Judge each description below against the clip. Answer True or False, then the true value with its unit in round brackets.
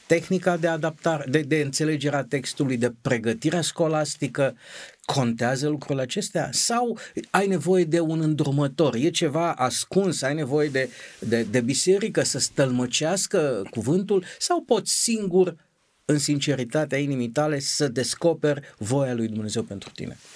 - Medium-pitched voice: True (150 Hz)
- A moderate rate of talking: True (135 wpm)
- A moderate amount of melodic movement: True (4.4 semitones)